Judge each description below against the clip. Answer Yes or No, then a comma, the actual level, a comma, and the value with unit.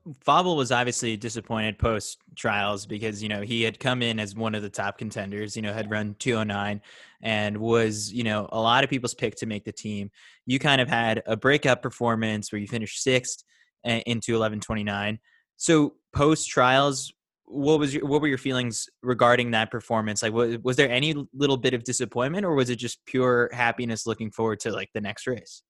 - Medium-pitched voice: No, low, 115 Hz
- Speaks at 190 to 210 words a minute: Yes, average, 200 wpm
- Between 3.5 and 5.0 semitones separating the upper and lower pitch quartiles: No, average, 2.9 semitones